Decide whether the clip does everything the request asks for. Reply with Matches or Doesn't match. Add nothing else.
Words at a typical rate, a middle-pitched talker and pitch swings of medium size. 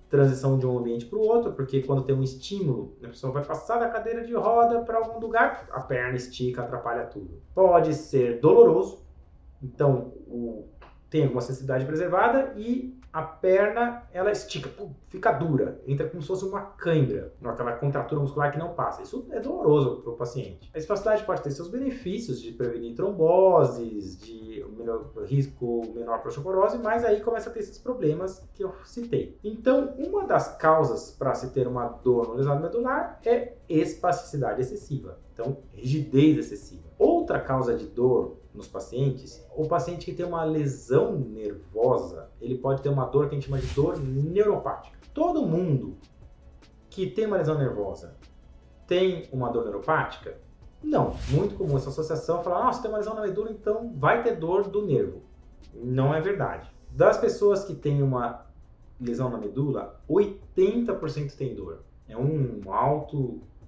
Doesn't match